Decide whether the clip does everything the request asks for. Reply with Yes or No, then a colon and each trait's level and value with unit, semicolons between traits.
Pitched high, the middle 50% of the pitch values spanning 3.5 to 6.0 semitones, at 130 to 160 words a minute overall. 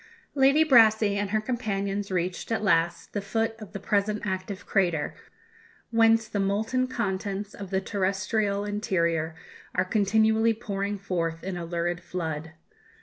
No: high, 200 Hz; average, 3.0 semitones; average, 145 wpm